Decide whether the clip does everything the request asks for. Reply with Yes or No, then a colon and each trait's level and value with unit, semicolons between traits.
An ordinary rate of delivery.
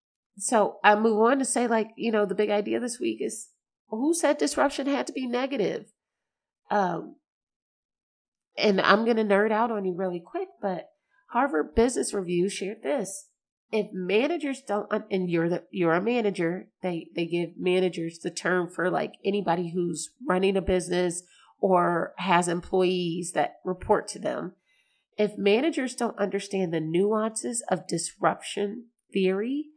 Yes: average, 155 wpm